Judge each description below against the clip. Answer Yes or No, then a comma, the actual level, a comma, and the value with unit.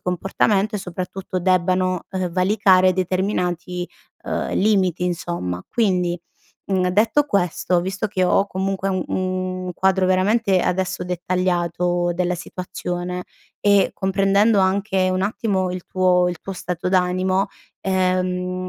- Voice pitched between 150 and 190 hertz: Yes, medium, 185 Hz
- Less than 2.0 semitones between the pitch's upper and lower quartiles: Yes, narrow, 1.2 semitones